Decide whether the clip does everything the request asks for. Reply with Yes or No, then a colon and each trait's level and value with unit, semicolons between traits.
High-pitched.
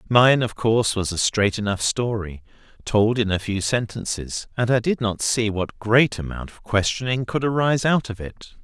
No: low, 110 Hz